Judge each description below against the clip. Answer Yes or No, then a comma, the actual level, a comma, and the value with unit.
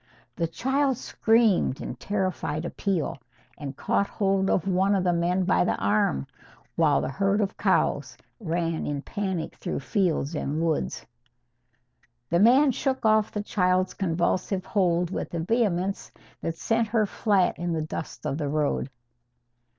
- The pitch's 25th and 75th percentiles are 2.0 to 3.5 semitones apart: No, average, 4.0 semitones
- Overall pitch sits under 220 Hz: Yes, medium, 185 Hz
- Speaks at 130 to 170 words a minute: Yes, average, 150 wpm